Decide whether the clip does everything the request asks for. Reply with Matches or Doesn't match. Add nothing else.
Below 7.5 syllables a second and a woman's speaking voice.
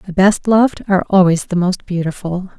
Matches